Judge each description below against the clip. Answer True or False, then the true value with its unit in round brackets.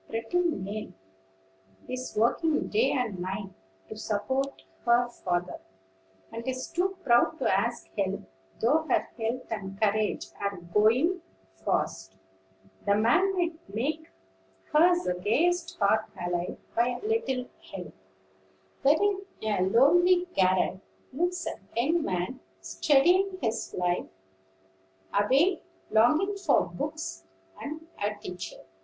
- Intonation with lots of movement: True (8.4 semitones)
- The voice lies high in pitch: True (235 Hz)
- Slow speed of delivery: True (120 wpm)